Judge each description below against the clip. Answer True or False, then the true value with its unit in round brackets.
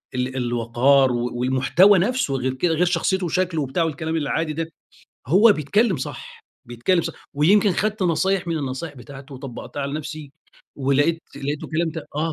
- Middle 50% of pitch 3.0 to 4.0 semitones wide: False (4.5 semitones)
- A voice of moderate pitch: True (155 Hz)